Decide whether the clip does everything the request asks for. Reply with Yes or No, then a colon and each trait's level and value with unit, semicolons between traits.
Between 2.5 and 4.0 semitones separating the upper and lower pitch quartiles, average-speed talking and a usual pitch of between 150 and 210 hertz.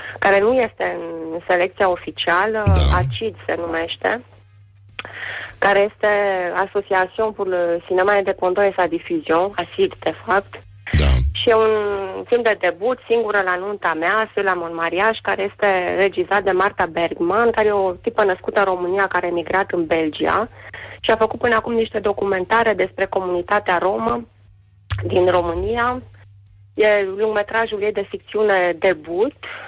Yes: average, 3.7 semitones; average, 140 wpm; high, 190 Hz